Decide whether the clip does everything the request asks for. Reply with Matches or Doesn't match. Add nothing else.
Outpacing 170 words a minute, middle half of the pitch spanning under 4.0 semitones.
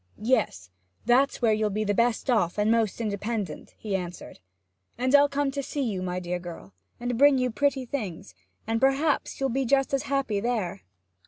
Doesn't match